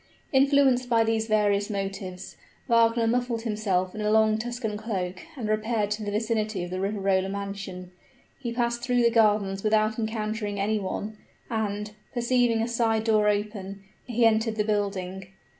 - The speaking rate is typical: Yes, average, 160 wpm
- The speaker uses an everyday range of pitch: No, narrow, 2.3 semitones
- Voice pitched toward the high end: Yes, high, 215 Hz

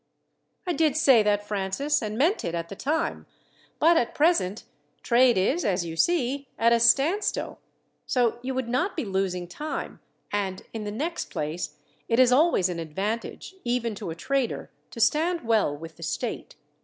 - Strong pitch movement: Yes, wide, 6.7 semitones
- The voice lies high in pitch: Yes, high, 235 Hz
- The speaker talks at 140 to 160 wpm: No, average, 175 wpm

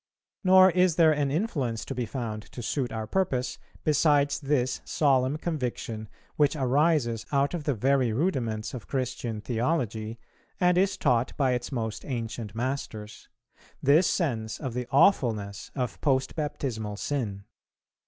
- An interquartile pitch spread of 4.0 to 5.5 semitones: Yes, average, 4.5 semitones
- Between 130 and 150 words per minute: Yes, average, 145 wpm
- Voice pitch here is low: Yes, low, 130 Hz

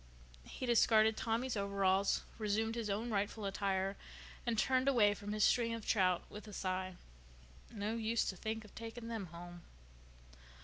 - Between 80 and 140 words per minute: No, average, 160 wpm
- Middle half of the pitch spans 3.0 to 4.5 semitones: No, narrow, 2.5 semitones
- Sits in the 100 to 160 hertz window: No, high, 215 Hz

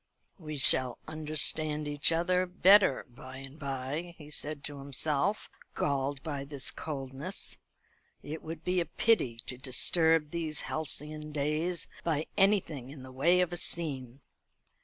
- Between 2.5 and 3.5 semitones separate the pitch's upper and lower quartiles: Yes, average, 3.2 semitones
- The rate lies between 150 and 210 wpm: No, average, 140 wpm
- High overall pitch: No, medium, 150 Hz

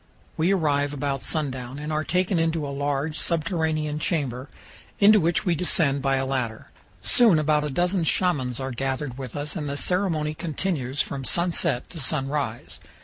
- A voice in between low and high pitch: Yes, medium, 150 Hz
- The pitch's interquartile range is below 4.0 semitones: Yes, average, 3.4 semitones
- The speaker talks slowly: No, average, 165 wpm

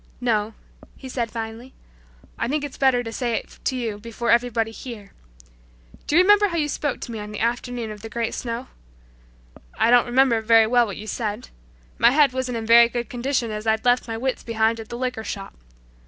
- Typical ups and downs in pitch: No, narrow, 2.1 semitones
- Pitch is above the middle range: Yes, high, 235 Hz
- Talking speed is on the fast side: Yes, fast, 210 wpm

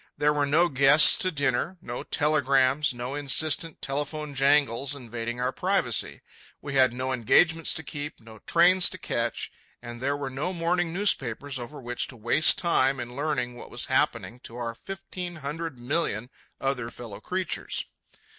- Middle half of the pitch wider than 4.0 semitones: Yes, average, 4.4 semitones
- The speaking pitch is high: No, medium, 140 Hz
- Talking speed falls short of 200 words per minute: Yes, average, 160 wpm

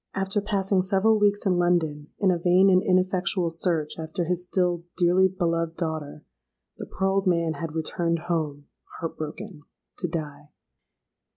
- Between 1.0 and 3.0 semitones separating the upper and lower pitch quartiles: Yes, average, 2.7 semitones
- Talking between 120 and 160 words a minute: Yes, average, 150 wpm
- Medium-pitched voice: Yes, medium, 175 Hz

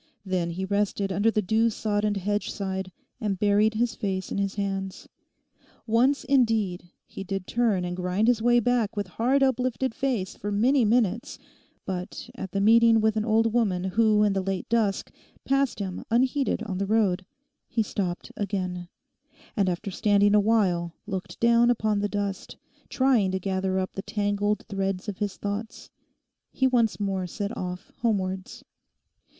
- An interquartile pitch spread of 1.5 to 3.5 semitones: Yes, average, 3.0 semitones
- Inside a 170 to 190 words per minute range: No, average, 160 wpm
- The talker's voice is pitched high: Yes, high, 205 Hz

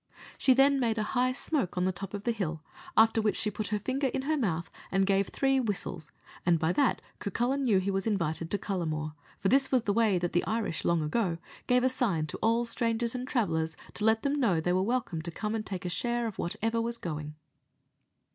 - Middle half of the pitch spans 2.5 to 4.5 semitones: No, average, 5.2 semitones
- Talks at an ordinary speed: No, fast, 225 wpm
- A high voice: Yes, high, 210 Hz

